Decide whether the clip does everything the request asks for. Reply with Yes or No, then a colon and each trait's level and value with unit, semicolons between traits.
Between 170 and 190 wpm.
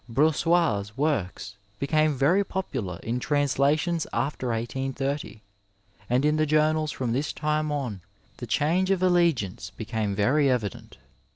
No: slow, 135 wpm